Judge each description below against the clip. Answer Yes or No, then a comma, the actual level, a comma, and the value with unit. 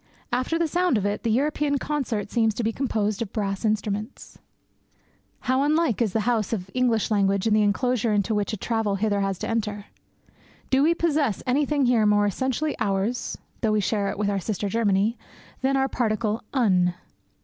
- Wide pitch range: No, average, 3.9 semitones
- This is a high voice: Yes, high, 220 Hz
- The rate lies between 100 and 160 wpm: No, average, 185 wpm